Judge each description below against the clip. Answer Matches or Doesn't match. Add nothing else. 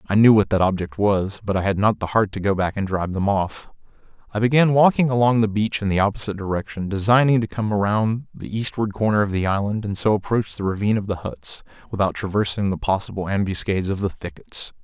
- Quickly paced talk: Matches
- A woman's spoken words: Doesn't match